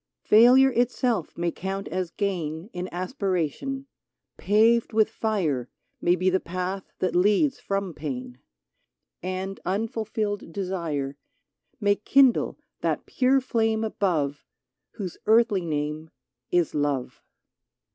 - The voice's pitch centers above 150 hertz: Yes, high, 190 Hz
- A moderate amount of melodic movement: Yes, average, 4.8 semitones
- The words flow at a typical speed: No, slow, 110 wpm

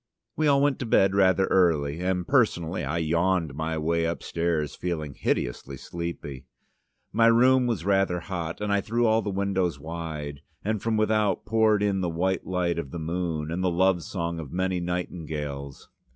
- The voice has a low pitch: Yes, very low, 90 Hz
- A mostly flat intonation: No, average, 3.6 semitones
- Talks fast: No, average, 175 wpm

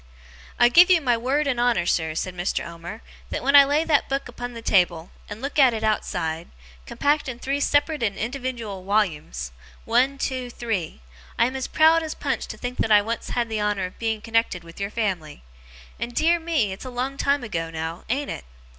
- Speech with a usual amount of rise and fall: No, wide, 6.1 semitones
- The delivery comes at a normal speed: No, fast, 210 wpm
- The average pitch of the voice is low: No, high, 235 Hz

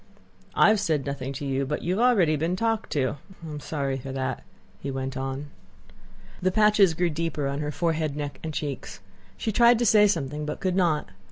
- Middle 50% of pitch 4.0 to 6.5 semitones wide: Yes, average, 5.1 semitones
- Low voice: No, medium, 150 Hz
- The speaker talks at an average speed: No, fast, 210 wpm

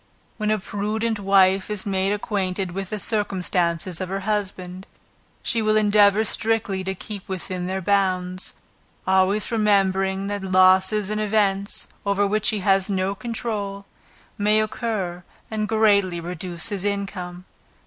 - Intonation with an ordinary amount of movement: No, narrow, 2.1 semitones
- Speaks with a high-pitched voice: Yes, high, 195 Hz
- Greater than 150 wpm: No, average, 140 wpm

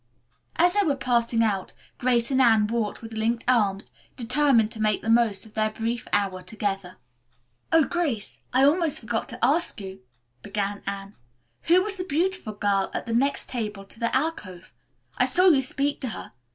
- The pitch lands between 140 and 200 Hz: No, high, 230 Hz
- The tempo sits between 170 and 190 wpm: Yes, average, 180 wpm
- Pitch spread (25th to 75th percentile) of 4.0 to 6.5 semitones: Yes, average, 5.2 semitones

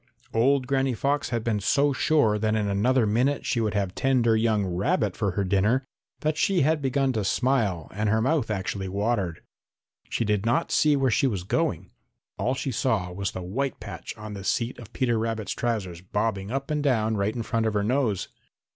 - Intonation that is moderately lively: Yes, average, 4.5 semitones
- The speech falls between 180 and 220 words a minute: Yes, average, 200 wpm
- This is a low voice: Yes, low, 115 Hz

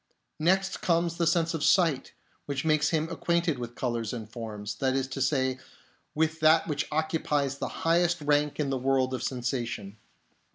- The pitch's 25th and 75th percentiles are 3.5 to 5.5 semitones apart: Yes, average, 4.0 semitones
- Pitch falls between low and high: Yes, medium, 145 Hz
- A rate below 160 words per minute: No, average, 170 wpm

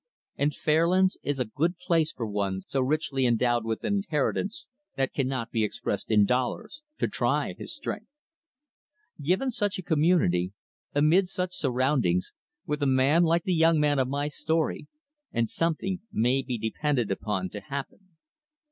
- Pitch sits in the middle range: Yes, medium, 145 Hz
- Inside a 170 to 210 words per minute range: No, average, 155 wpm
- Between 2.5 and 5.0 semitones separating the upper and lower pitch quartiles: No, wide, 5.6 semitones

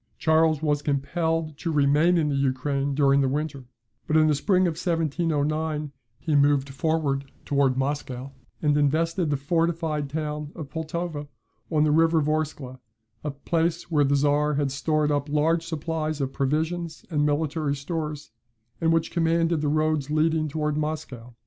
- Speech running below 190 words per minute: Yes, average, 155 wpm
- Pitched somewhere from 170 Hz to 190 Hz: No, medium, 150 Hz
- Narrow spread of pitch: Yes, narrow, 2.1 semitones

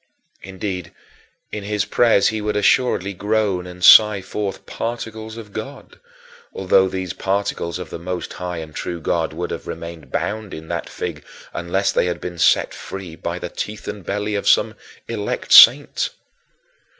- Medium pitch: No, very low, 95 Hz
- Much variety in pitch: No, average, 3.0 semitones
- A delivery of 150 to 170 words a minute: Yes, average, 160 wpm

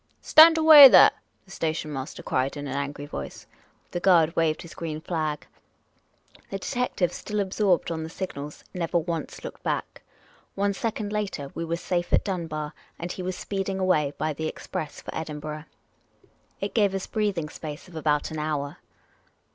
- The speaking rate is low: No, average, 170 wpm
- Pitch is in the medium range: Yes, medium, 165 Hz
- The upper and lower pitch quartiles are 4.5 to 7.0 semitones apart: No, average, 4.1 semitones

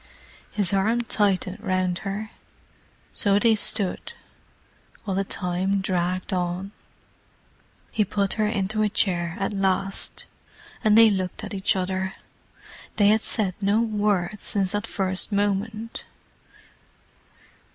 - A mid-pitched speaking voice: No, high, 195 Hz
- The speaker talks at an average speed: No, slow, 120 wpm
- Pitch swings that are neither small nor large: No, narrow, 2.1 semitones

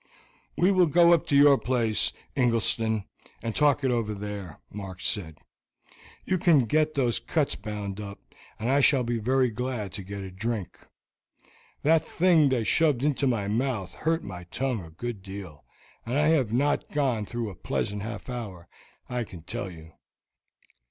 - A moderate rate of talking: Yes, average, 170 wpm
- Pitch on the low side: Yes, low, 115 Hz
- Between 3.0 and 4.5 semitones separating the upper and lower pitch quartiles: No, wide, 5.5 semitones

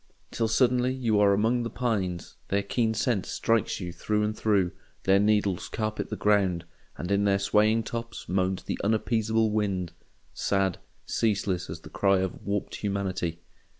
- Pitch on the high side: No, low, 105 Hz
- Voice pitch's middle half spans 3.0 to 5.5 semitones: No, narrow, 2.6 semitones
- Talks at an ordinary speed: Yes, average, 160 wpm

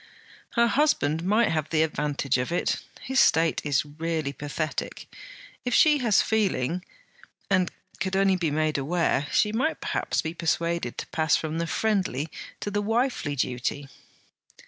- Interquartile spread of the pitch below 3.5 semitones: No, wide, 5.6 semitones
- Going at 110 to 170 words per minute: Yes, average, 150 wpm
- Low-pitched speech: No, medium, 165 Hz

